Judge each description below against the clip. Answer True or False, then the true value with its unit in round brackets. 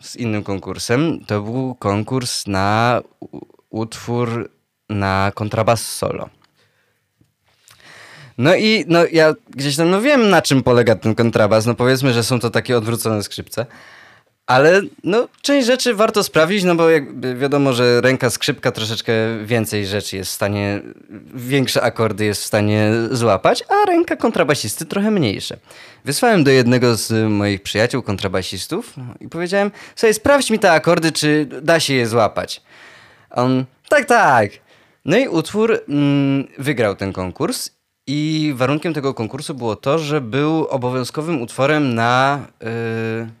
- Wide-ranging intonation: True (5.9 semitones)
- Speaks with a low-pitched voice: True (130 Hz)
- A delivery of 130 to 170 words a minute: True (145 wpm)